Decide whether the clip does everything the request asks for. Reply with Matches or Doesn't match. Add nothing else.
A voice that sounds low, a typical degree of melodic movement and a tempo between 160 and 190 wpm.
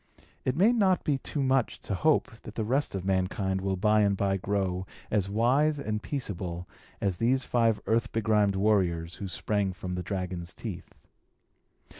Matches